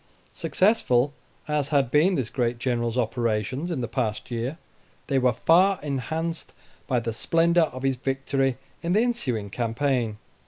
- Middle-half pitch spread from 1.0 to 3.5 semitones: No, average, 5.0 semitones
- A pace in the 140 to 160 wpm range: Yes, average, 150 wpm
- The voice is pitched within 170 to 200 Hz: No, low, 135 Hz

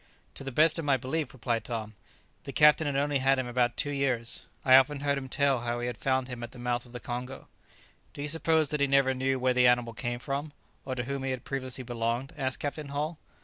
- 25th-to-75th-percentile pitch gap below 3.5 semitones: Yes, narrow, 2.5 semitones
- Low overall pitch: Yes, low, 130 Hz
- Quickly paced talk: Yes, fast, 240 wpm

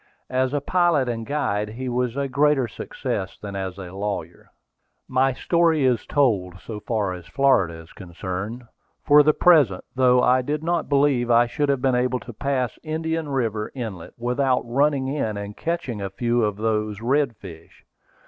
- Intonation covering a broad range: No, average, 5.0 semitones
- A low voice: Yes, low, 125 Hz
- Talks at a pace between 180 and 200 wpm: No, average, 165 wpm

